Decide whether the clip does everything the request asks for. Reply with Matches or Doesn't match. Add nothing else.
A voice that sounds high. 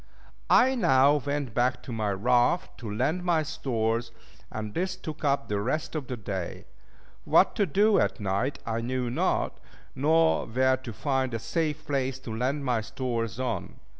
Doesn't match